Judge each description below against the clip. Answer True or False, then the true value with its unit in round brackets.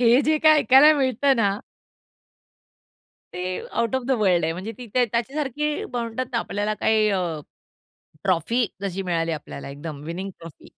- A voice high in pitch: True (225 Hz)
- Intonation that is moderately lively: False (6.2 semitones)